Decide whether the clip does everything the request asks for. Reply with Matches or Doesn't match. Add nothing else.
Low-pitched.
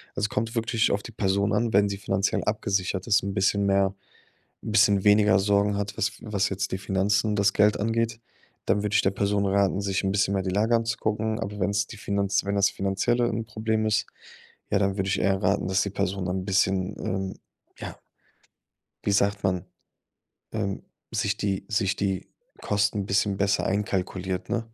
Matches